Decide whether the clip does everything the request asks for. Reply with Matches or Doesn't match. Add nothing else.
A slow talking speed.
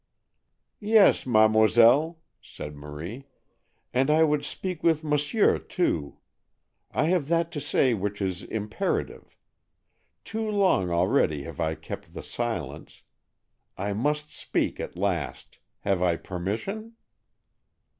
Matches